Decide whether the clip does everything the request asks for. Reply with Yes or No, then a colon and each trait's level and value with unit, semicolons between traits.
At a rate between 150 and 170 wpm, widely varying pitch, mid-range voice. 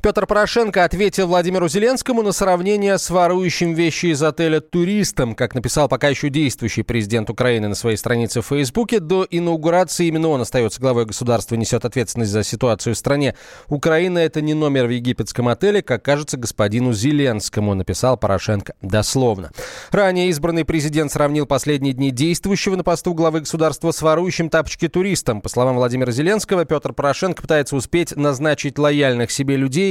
Yes: fast, 160 wpm; wide, 5.9 semitones; medium, 145 Hz